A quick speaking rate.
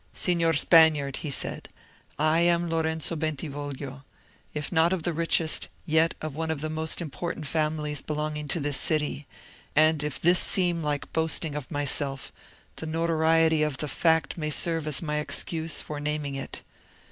No: average, 160 wpm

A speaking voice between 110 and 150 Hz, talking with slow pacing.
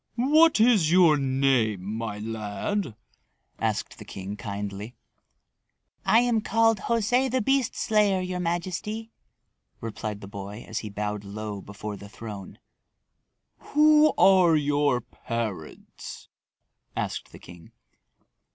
Yes: low, 135 Hz; slow, 115 wpm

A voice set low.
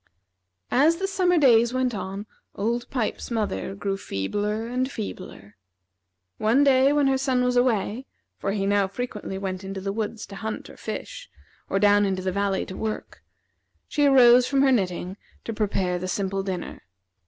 No: high, 215 Hz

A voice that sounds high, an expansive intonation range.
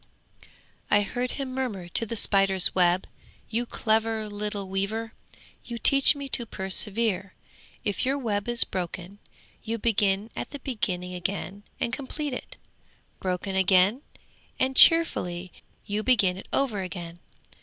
No: high, 205 Hz; average, 4.0 semitones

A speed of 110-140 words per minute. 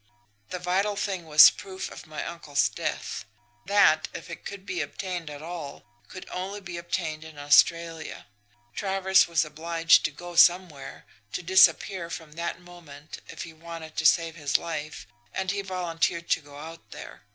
No: average, 165 wpm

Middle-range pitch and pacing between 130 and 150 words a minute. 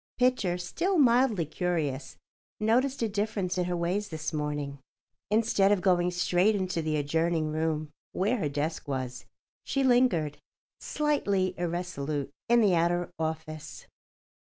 Yes: medium, 175 Hz; slow, 135 wpm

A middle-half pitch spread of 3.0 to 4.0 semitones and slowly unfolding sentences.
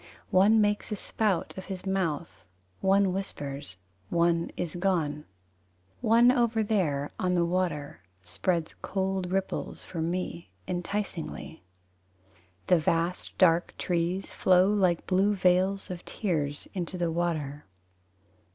No: narrow, 2.5 semitones; slow, 120 wpm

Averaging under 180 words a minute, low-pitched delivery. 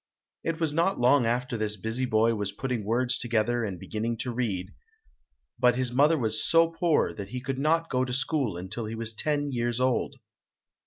No: average, 195 wpm; low, 120 Hz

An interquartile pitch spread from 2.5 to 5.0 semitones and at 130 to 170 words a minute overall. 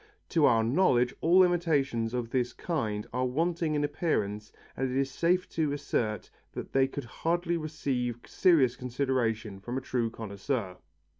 No: wide, 5.4 semitones; average, 155 wpm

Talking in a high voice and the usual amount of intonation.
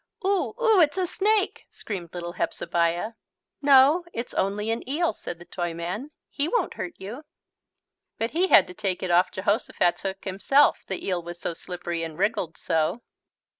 No: high, 200 Hz; wide, 8.8 semitones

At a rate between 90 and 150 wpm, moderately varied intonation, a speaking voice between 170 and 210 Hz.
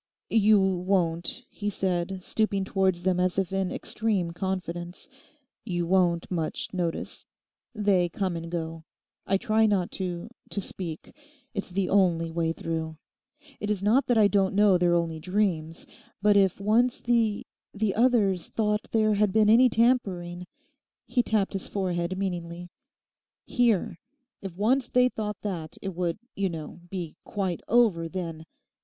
Yes: average, 140 wpm; average, 3.3 semitones; high, 190 Hz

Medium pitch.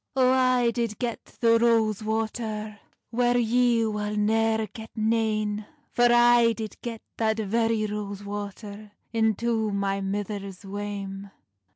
No: high, 220 Hz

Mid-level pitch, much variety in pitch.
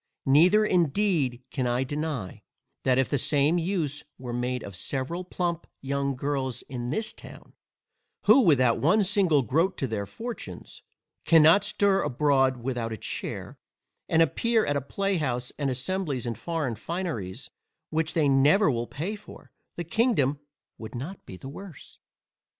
Yes: medium, 145 Hz; wide, 5.8 semitones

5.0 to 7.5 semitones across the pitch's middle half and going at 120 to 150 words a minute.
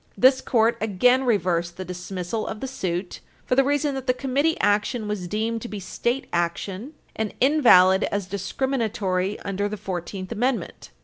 No: average, 5.3 semitones; average, 165 wpm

